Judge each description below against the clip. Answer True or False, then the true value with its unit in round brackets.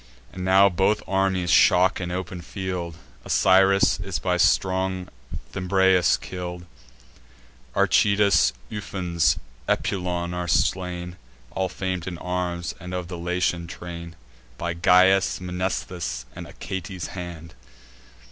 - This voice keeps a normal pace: False (110 wpm)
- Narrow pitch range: True (1.3 semitones)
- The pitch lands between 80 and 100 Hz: True (90 Hz)